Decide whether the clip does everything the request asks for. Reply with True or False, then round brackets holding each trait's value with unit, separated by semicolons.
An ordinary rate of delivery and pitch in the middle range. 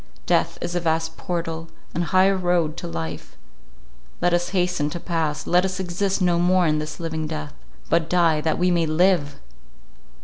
True (175 wpm; 170 Hz)